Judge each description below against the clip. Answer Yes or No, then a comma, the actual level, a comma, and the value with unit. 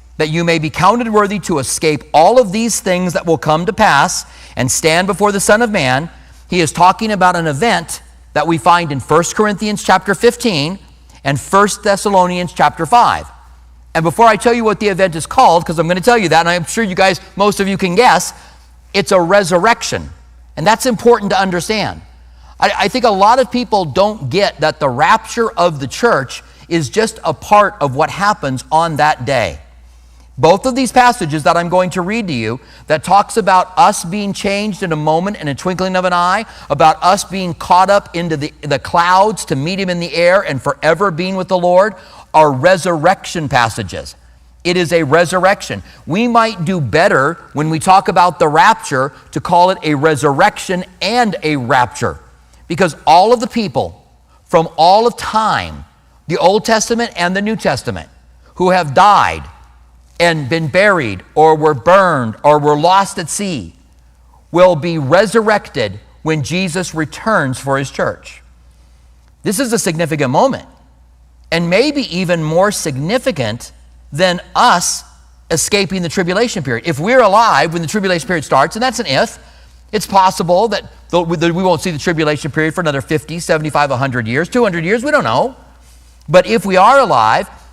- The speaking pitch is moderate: Yes, medium, 175 Hz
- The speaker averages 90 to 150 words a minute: No, average, 185 wpm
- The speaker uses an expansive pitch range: Yes, wide, 6.1 semitones